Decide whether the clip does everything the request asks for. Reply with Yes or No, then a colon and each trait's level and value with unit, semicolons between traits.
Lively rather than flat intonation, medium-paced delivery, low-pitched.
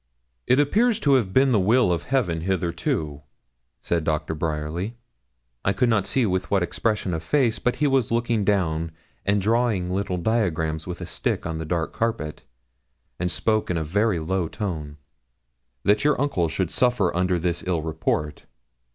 Yes: wide, 5.7 semitones; average, 170 wpm; very low, 95 Hz